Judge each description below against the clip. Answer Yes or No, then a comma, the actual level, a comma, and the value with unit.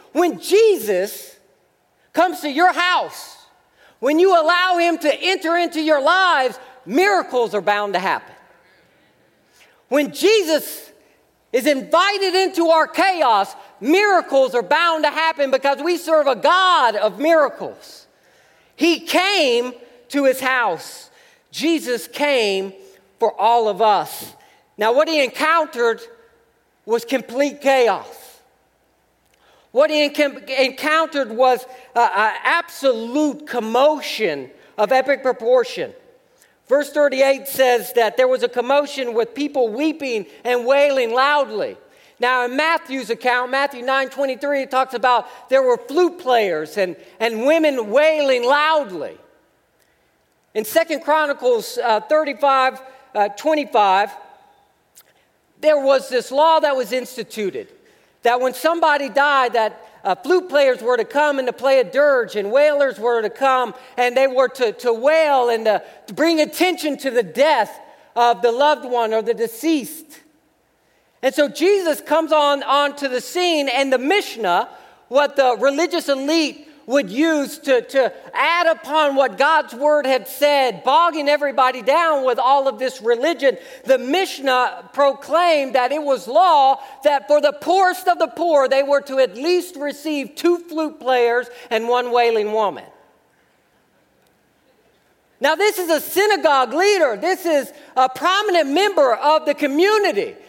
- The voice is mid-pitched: No, very high, 280 Hz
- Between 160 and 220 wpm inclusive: No, average, 140 wpm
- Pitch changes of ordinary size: Yes, average, 4.2 semitones